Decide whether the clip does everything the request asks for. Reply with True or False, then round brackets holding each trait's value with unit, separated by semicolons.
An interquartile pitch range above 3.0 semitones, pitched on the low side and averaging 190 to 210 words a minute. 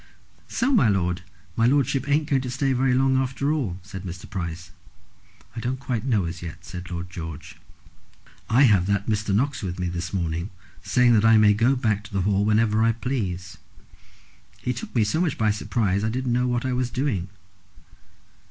True (5.4 semitones; 110 Hz; 195 wpm)